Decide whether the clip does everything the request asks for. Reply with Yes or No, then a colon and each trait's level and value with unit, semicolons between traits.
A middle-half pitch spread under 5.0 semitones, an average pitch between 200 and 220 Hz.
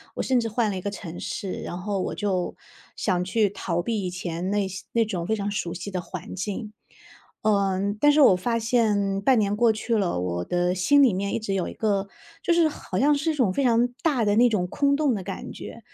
Yes: average, 3.9 semitones; high, 205 Hz